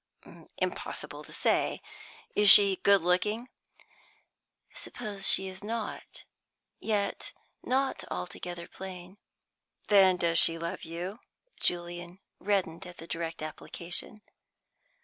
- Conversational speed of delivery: No, slow, 105 wpm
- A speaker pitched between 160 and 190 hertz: Yes, medium, 185 Hz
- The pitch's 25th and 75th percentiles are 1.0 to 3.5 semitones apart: Yes, average, 2.9 semitones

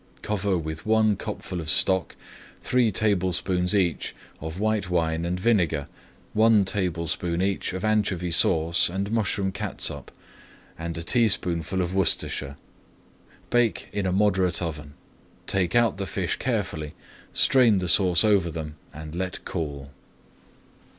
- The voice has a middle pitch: No, very low, 90 Hz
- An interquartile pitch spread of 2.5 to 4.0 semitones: Yes, average, 3.6 semitones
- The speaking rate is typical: No, slow, 130 wpm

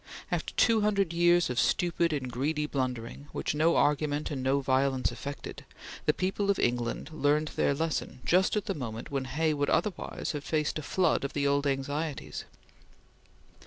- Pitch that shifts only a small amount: No, average, 3.4 semitones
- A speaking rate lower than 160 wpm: No, average, 170 wpm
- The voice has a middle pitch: Yes, medium, 145 Hz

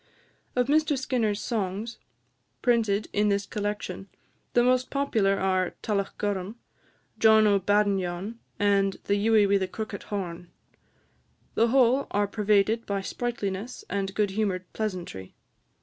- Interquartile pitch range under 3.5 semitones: Yes, narrow, 2.6 semitones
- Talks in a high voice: Yes, high, 205 Hz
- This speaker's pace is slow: Yes, slow, 125 wpm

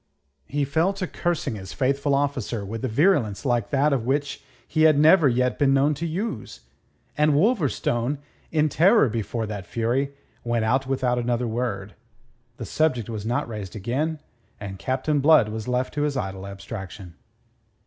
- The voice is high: No, low, 130 Hz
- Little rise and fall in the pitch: No, average, 4.9 semitones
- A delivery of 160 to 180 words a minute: Yes, average, 165 wpm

